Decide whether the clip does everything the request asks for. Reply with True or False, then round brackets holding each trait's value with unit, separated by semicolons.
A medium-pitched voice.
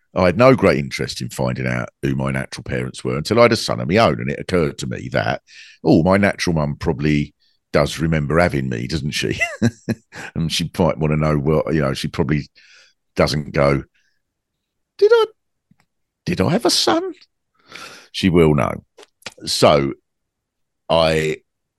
False (80 Hz)